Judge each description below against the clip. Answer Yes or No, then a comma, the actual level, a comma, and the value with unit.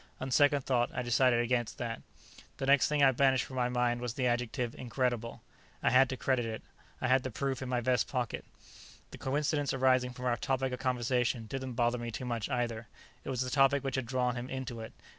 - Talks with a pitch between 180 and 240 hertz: No, low, 125 Hz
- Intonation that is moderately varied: No, narrow, 1.7 semitones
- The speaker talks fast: Yes, fast, 220 wpm